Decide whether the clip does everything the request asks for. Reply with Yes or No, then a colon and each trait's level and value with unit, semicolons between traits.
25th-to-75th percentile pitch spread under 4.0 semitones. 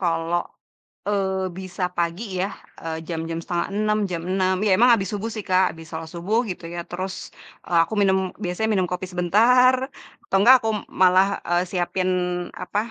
Yes: average, 2.7 semitones